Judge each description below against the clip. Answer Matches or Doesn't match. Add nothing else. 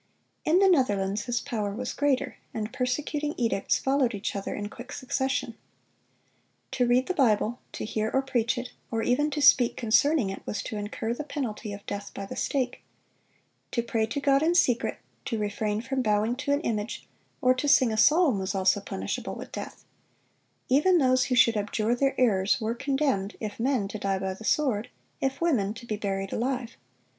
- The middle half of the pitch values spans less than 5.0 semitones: Matches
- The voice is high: Matches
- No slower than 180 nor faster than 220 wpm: Matches